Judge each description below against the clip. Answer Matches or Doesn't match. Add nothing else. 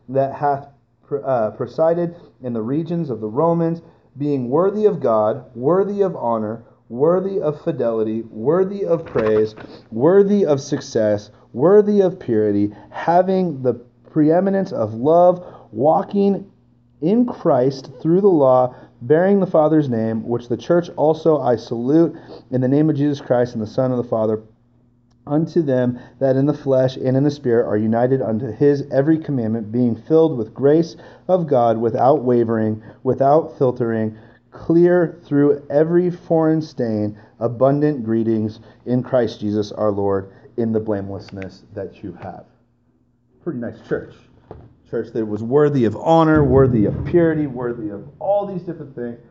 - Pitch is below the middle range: Matches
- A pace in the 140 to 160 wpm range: Matches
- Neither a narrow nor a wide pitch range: Doesn't match